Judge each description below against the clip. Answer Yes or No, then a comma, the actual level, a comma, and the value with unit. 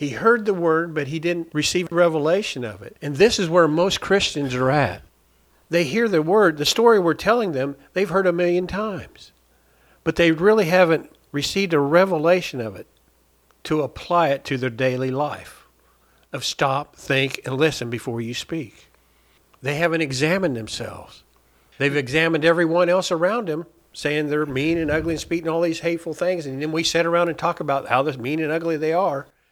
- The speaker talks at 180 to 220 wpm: Yes, average, 190 wpm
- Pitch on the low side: No, medium, 160 Hz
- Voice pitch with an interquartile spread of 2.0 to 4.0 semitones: No, average, 4.5 semitones